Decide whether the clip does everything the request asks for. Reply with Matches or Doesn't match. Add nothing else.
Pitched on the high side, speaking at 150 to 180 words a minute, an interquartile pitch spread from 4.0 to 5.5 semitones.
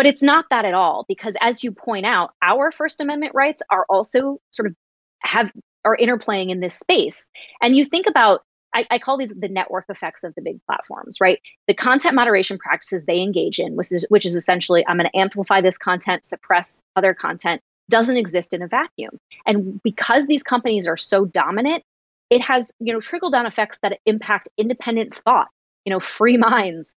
Doesn't match